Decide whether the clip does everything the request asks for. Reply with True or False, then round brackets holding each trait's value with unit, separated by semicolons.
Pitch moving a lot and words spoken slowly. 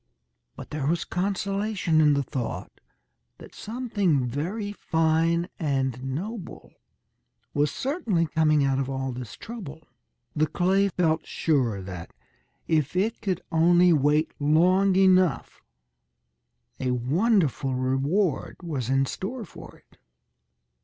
True (5.7 semitones; 120 wpm)